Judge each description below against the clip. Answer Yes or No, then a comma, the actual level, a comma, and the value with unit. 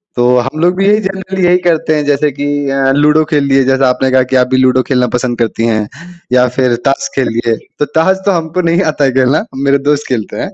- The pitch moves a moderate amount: Yes, average, 3.8 semitones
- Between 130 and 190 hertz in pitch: Yes, low, 135 Hz